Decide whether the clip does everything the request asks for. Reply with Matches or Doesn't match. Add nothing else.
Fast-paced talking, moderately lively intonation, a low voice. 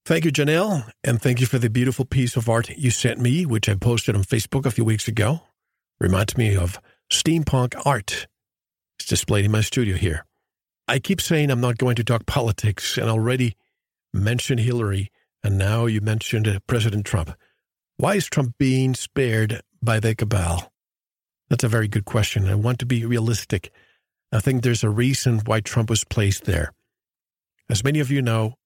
Doesn't match